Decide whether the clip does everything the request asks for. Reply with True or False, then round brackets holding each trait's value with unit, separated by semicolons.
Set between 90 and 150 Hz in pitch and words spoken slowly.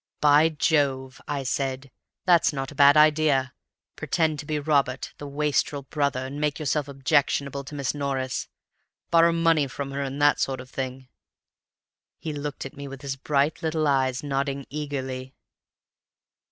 False (140 Hz; 155 wpm)